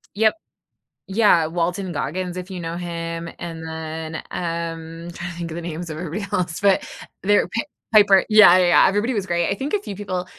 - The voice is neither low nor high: Yes, medium, 175 Hz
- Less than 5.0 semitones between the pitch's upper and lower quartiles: Yes, average, 2.8 semitones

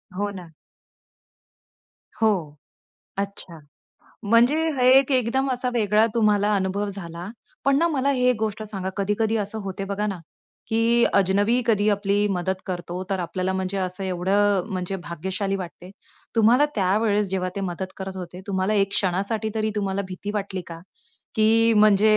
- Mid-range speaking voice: No, high, 200 Hz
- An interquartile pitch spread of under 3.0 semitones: Yes, narrow, 2.5 semitones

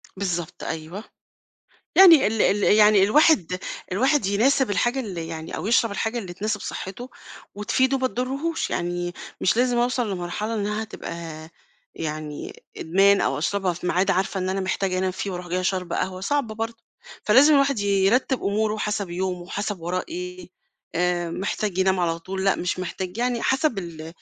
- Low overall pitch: No, high, 200 Hz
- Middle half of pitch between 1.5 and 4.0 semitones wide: No, average, 4.4 semitones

